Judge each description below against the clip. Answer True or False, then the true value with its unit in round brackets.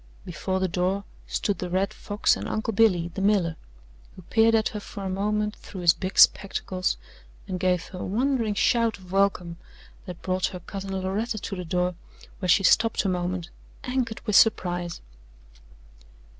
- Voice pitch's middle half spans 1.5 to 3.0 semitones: True (2.7 semitones)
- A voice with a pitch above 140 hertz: True (190 Hz)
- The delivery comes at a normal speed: True (170 wpm)